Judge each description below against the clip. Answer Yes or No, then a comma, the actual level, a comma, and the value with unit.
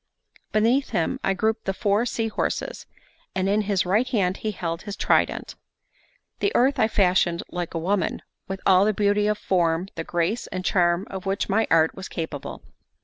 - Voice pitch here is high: Yes, high, 195 Hz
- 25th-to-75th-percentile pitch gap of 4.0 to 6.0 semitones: No, average, 3.2 semitones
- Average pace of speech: Yes, average, 185 wpm